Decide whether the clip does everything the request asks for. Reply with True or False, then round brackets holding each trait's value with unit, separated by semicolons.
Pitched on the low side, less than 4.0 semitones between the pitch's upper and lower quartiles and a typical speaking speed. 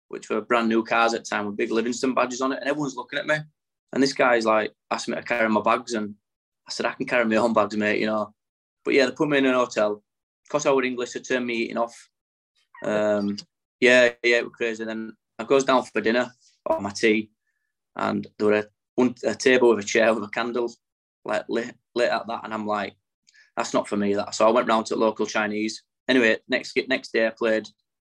False (115 Hz; 2.8 semitones; 245 wpm)